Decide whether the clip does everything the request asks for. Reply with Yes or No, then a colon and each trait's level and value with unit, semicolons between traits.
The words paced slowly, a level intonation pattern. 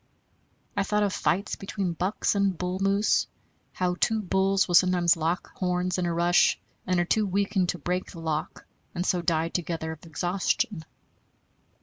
No: average, 165 wpm; narrow, 2.2 semitones